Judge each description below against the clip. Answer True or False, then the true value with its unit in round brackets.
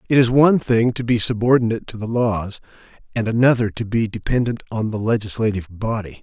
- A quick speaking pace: False (185 wpm)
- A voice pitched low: True (115 Hz)